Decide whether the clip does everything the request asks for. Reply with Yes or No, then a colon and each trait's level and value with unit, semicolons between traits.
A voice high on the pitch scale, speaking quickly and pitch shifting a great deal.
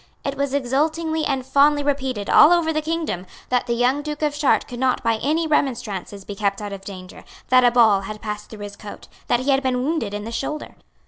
Yes: very high, 255 Hz; fast, 225 wpm; wide, 5.8 semitones